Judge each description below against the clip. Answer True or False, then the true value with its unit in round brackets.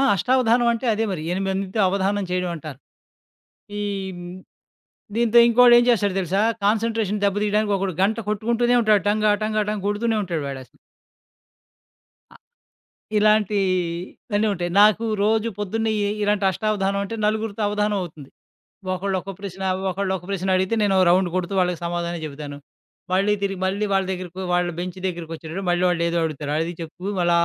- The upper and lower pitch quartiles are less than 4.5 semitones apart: True (3.1 semitones)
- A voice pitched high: True (195 Hz)